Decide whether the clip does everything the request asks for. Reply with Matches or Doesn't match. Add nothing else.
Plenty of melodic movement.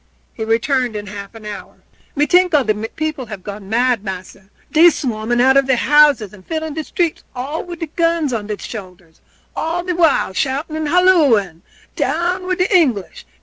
Matches